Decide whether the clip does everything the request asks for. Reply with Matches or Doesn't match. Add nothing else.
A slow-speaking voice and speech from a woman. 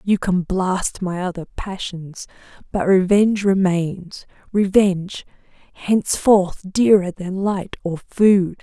Matches